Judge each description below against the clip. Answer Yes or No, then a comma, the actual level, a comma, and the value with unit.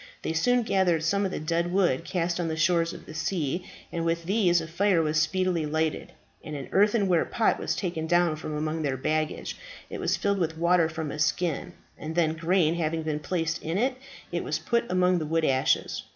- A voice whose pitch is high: No, medium, 165 Hz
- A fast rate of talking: Yes, fast, 210 wpm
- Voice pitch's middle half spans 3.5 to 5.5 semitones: No, narrow, 2.5 semitones